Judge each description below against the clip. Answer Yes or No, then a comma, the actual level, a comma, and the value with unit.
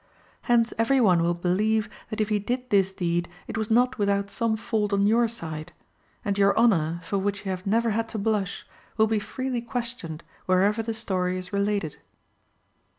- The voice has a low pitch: No, high, 205 Hz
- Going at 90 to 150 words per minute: No, average, 185 wpm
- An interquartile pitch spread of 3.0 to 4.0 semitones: Yes, average, 3.4 semitones